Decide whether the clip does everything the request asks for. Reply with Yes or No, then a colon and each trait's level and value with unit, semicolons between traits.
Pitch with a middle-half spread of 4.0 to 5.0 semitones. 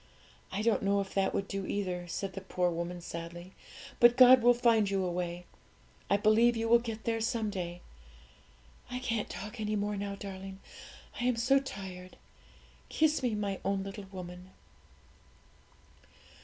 No: average, 3.6 semitones